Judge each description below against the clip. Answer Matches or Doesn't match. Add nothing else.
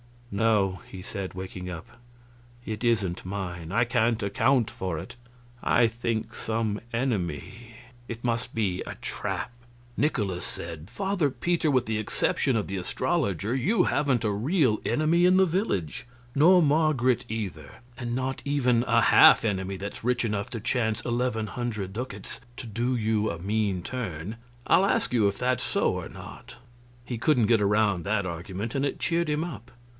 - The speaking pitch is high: Doesn't match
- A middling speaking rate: Matches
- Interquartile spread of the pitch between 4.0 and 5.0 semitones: Matches